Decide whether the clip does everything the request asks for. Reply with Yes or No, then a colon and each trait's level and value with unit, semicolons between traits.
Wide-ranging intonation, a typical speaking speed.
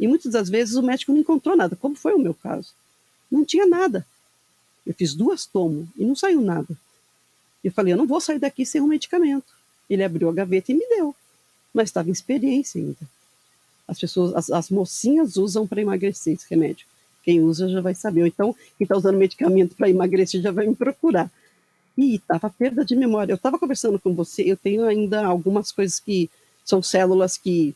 No: wide, 6.6 semitones; fast, 200 wpm